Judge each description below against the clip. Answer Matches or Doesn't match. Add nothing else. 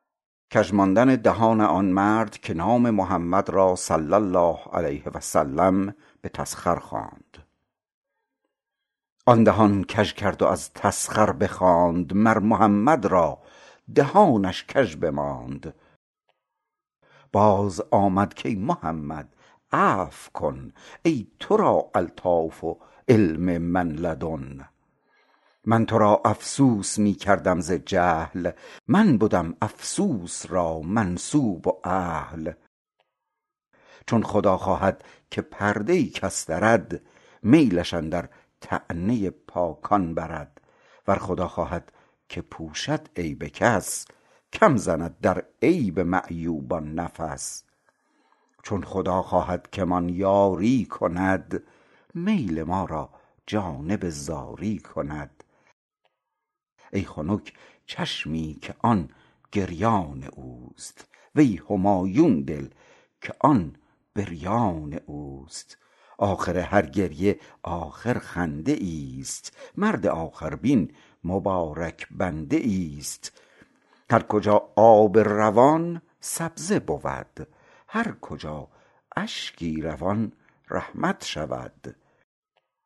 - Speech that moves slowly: Matches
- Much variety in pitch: Doesn't match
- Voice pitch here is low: Matches